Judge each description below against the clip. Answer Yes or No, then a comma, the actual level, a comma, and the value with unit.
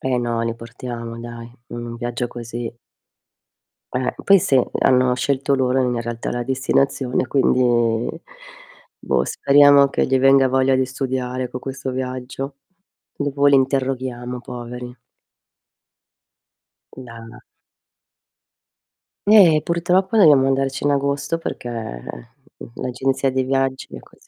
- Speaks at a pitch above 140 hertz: No, low, 130 Hz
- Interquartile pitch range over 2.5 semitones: No, narrow, 1.9 semitones